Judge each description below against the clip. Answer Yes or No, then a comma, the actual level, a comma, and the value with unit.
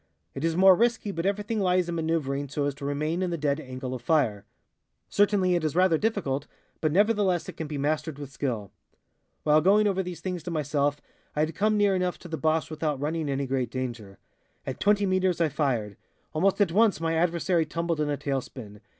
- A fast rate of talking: Yes, fast, 210 wpm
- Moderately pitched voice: Yes, medium, 160 Hz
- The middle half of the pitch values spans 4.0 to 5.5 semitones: Yes, average, 4.6 semitones